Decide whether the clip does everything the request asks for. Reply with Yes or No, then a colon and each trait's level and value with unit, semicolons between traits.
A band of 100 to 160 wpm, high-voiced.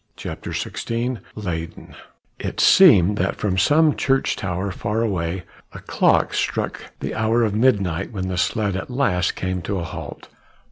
No: average, 155 wpm; low, 100 Hz